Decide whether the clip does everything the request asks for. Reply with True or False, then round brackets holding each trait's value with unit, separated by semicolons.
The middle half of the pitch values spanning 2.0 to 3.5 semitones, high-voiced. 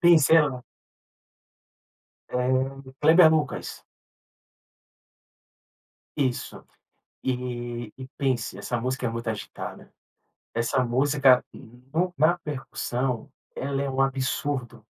False (2.7 semitones; 130 Hz)